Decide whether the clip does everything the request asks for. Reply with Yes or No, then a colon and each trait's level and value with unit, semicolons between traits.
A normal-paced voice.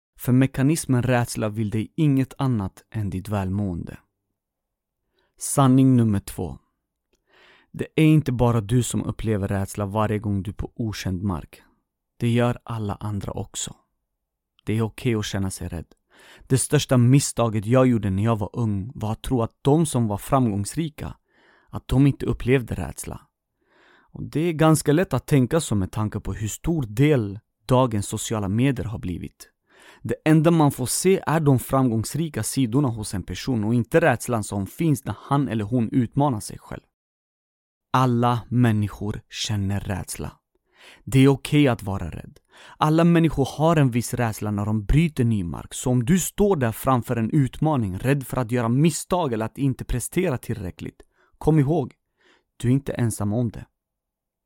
Yes: average, 170 wpm